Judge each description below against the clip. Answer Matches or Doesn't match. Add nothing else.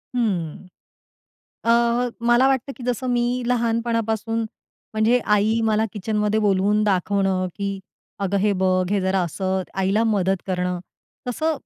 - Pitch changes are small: Doesn't match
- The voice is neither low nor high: Doesn't match